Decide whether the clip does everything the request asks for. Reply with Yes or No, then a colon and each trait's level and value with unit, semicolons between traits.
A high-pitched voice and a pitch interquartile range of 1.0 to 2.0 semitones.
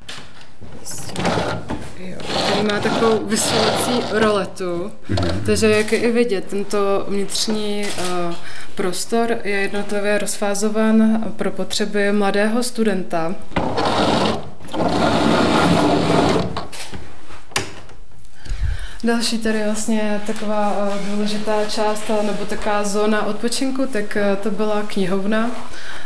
Yes: high, 210 Hz; narrow, 1.7 semitones